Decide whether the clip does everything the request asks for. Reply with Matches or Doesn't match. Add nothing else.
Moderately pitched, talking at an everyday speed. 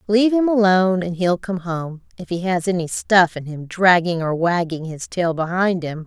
Doesn't match